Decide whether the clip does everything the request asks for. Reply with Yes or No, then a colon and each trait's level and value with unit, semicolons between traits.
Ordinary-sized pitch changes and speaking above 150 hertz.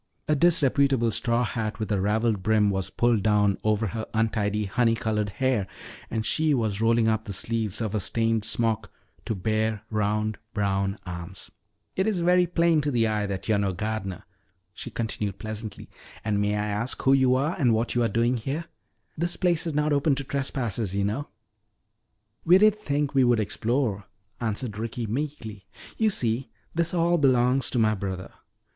No: average, 4.4 semitones; low, 115 Hz